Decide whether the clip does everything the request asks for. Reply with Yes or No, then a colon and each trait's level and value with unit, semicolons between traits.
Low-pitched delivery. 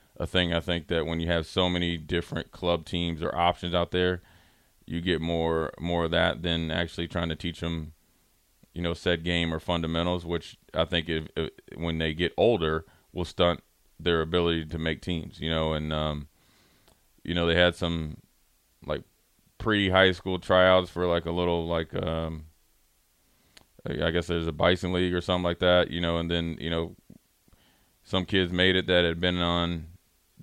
Yes: very low, 85 Hz